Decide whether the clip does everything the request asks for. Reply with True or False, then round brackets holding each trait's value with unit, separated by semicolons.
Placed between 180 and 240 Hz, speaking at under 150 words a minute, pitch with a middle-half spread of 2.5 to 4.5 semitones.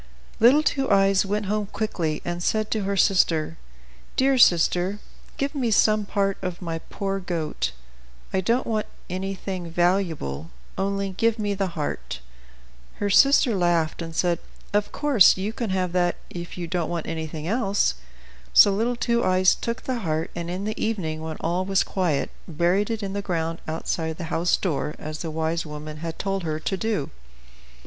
False (185 Hz; 175 wpm; 3.9 semitones)